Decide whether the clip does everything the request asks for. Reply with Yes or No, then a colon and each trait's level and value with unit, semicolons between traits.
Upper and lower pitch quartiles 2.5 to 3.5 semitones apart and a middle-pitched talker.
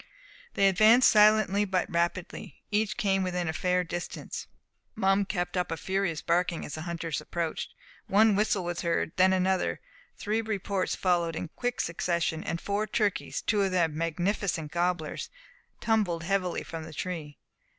Yes: average, 3.0 semitones; medium, 180 Hz